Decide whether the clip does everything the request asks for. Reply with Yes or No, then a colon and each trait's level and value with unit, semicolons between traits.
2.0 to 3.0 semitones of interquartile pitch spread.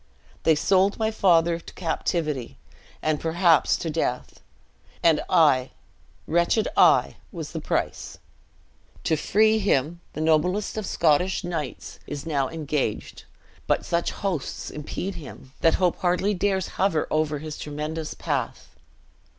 No: average, 3.5 semitones